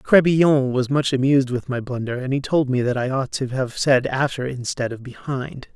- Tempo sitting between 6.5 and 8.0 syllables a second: No, 5.1 syllables/s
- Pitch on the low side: Yes, low, 130 Hz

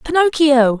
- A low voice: No, very high, 290 Hz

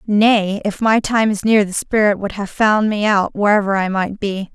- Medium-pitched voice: No, high, 205 Hz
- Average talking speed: No, fast, 225 wpm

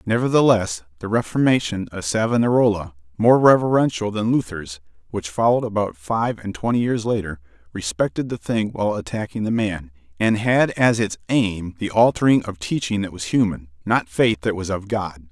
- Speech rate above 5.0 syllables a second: Yes, 5.2 syllables/s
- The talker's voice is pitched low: Yes, low, 105 Hz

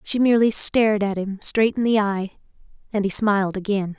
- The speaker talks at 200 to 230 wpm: No, average, 180 wpm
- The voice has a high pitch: Yes, high, 205 Hz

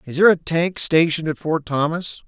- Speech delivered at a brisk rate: Yes, fast, 210 wpm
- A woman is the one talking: No, male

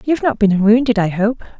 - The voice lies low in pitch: No, high, 225 Hz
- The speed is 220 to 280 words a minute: Yes, fast, 265 wpm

